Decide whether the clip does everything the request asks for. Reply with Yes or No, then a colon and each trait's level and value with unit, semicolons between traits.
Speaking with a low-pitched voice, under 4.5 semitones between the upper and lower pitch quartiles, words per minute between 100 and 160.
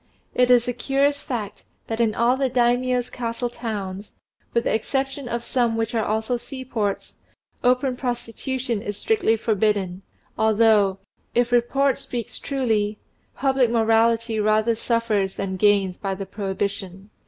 No: high, 230 Hz; average, 3.0 semitones; average, 140 wpm